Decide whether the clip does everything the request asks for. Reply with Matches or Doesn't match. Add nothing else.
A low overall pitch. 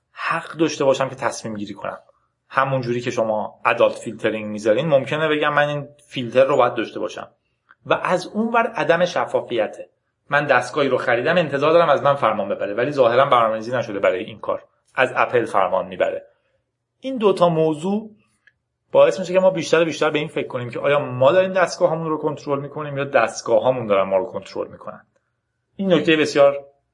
Doesn't match